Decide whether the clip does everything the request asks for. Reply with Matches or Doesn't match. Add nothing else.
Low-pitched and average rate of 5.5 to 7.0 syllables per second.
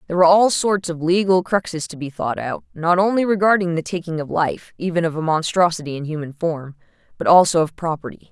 Doesn't match